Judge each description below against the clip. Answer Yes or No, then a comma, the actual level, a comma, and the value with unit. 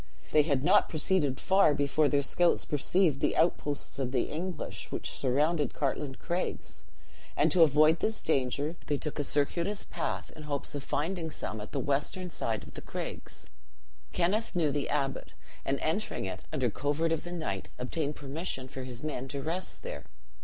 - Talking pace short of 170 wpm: No, average, 175 wpm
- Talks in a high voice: No, medium, 150 Hz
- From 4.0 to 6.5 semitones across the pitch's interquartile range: No, average, 3.6 semitones